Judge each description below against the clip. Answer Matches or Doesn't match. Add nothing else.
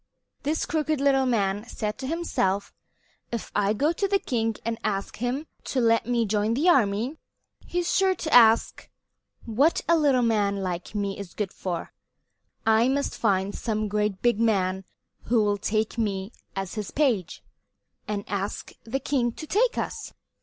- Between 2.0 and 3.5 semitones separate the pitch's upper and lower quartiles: Doesn't match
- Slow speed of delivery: Doesn't match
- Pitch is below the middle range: Doesn't match